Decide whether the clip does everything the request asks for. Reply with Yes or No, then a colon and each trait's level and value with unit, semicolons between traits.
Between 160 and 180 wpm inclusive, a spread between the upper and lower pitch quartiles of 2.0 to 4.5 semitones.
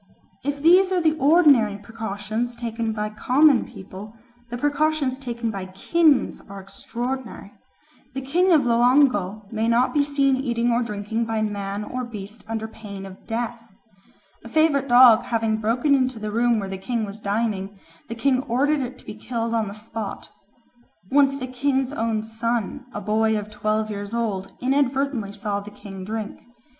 Yes: average, 170 wpm; average, 3.8 semitones